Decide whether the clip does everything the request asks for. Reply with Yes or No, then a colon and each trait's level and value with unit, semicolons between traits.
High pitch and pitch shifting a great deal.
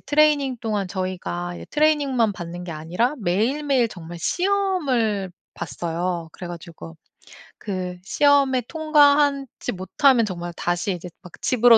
Yes: high, 215 Hz; wide, 8.1 semitones